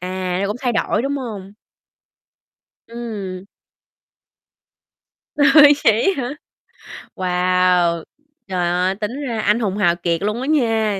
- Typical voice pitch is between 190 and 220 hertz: Yes, high, 205 Hz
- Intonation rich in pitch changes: No, average, 4.6 semitones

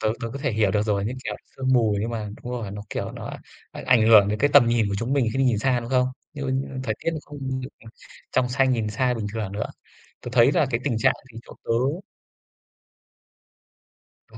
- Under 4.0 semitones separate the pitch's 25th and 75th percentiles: Yes, average, 3.4 semitones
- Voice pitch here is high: No, low, 120 Hz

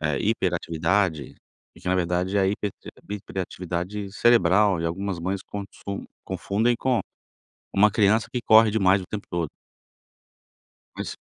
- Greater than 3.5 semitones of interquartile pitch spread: No, average, 2.8 semitones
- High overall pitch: No, low, 100 Hz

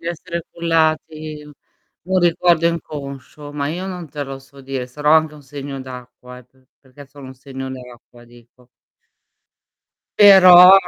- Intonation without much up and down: No, average, 4.0 semitones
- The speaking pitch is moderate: Yes, medium, 145 Hz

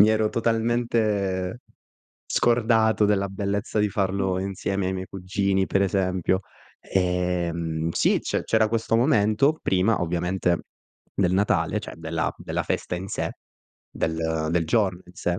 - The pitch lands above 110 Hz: No, very low, 95 Hz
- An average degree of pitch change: Yes, average, 3.2 semitones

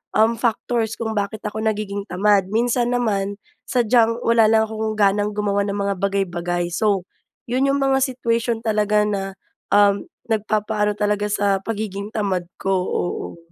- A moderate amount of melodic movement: No, narrow, 2.1 semitones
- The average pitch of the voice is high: Yes, high, 210 Hz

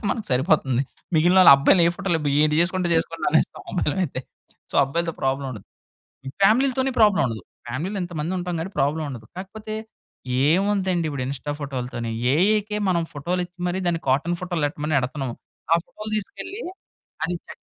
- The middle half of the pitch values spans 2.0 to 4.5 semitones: No, average, 5.1 semitones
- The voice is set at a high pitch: No, medium, 170 Hz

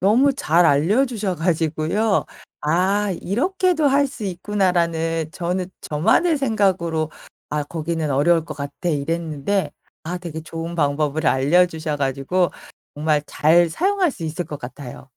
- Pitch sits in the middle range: Yes, medium, 170 Hz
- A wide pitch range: No, average, 4.5 semitones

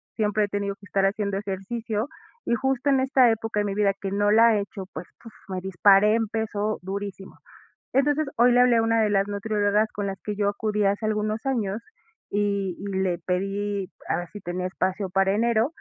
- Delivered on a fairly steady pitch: Yes, narrow, 2.2 semitones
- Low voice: No, high, 205 Hz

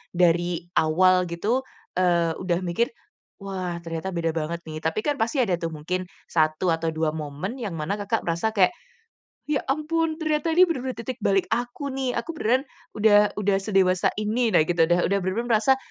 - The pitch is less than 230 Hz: Yes, high, 190 Hz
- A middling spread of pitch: No, wide, 5.9 semitones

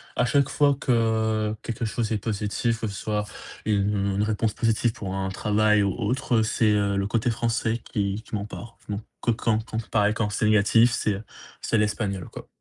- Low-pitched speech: Yes, low, 110 Hz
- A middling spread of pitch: No, narrow, 1.8 semitones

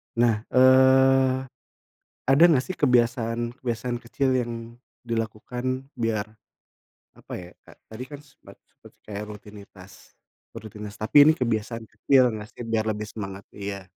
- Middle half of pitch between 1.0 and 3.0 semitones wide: No, average, 3.4 semitones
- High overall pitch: No, low, 115 Hz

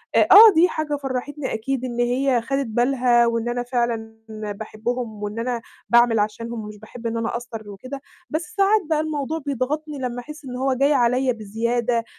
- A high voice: Yes, high, 245 Hz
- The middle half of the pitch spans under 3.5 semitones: Yes, average, 3.0 semitones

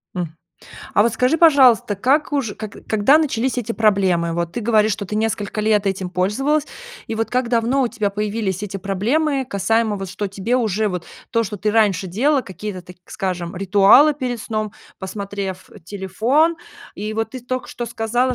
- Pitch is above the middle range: Yes, high, 215 Hz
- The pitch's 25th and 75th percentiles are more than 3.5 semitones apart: Yes, average, 4.0 semitones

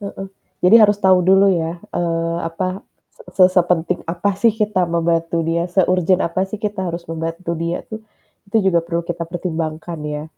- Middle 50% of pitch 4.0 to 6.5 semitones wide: No, narrow, 2.4 semitones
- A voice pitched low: No, medium, 175 Hz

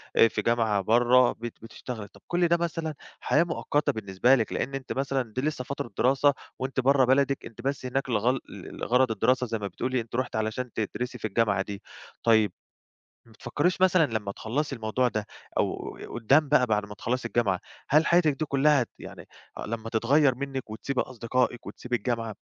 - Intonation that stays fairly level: No, average, 3.5 semitones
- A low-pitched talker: Yes, low, 125 Hz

